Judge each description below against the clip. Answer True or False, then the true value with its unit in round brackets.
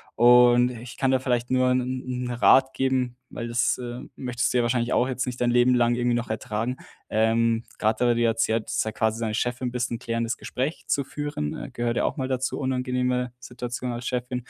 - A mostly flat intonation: True (1.3 semitones)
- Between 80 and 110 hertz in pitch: False (125 Hz)